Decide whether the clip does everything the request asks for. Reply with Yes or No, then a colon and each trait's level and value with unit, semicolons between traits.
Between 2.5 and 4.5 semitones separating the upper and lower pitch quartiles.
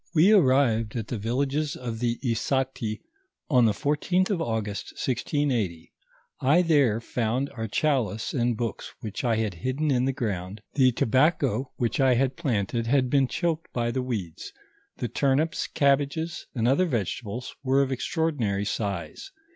Yes: average, 4.0 semitones